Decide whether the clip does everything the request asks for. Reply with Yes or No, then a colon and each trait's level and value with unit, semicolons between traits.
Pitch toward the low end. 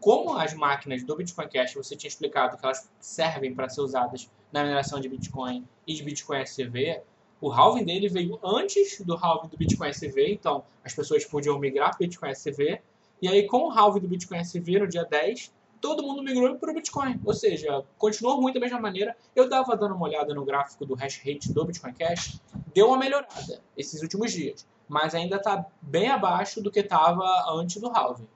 No: medium, 175 Hz